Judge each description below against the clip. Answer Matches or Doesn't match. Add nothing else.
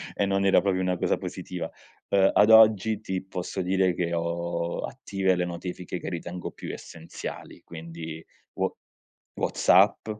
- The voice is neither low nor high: Doesn't match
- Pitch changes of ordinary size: Doesn't match